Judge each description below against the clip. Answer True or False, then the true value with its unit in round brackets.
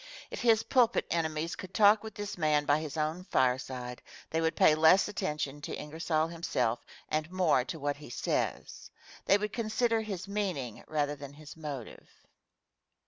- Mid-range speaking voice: True (160 Hz)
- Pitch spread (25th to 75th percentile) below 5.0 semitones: False (5.3 semitones)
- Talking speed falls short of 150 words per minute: False (165 wpm)